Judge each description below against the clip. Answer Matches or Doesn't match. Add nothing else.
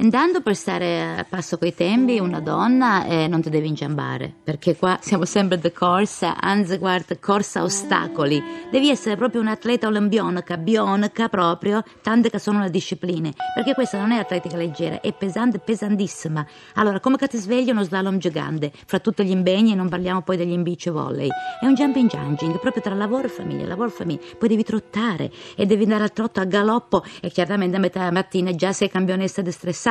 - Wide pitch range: Doesn't match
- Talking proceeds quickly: Matches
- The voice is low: Doesn't match